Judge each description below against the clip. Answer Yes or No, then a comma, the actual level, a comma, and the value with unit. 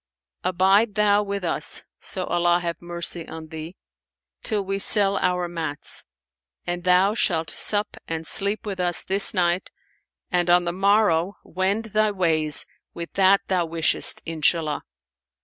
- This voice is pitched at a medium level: Yes, medium, 180 Hz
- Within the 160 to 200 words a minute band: No, average, 145 wpm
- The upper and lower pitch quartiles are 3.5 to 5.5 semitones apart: No, average, 2.8 semitones